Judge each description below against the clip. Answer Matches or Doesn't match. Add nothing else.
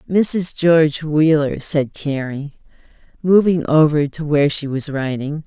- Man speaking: Doesn't match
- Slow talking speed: Matches